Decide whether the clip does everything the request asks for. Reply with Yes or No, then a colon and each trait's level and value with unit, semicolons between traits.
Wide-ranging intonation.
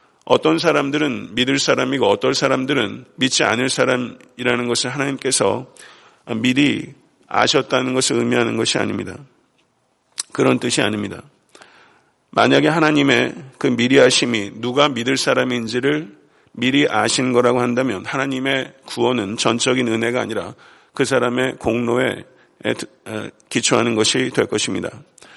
No: narrow, 2.2 semitones